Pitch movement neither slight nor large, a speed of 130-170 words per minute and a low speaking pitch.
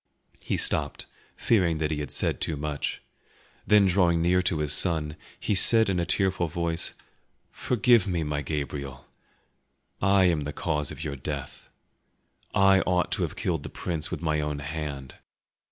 Yes: average, 3.7 semitones; average, 165 wpm; very low, 80 Hz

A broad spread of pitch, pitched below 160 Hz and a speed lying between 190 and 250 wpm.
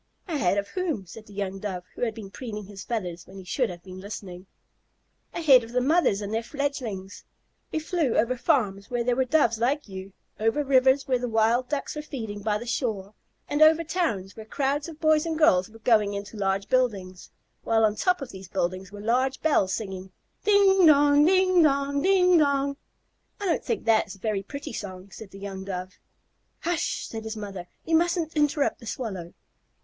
No: wide, 6.7 semitones; high, 230 Hz; average, 200 wpm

